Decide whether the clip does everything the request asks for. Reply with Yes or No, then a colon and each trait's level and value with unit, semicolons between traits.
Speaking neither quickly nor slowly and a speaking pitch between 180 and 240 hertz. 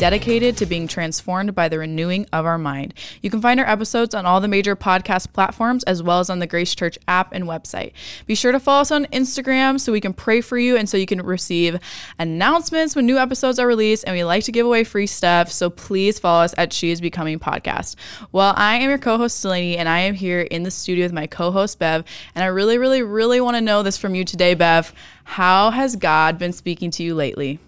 No: fast, 245 wpm; high, 190 Hz